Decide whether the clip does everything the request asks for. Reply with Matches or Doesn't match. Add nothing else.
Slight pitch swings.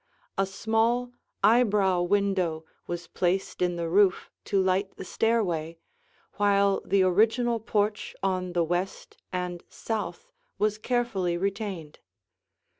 Doesn't match